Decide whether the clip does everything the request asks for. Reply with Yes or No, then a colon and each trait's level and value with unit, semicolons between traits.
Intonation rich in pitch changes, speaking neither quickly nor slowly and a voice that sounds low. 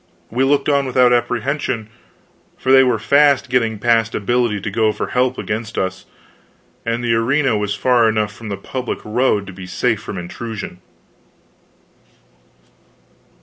No: average, 3.2 semitones; average, 150 wpm; low, 115 Hz